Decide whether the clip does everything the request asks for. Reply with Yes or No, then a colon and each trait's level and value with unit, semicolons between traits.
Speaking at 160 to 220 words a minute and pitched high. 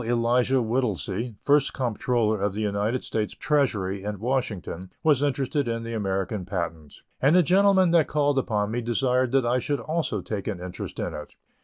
No: average, 175 wpm; low, 120 Hz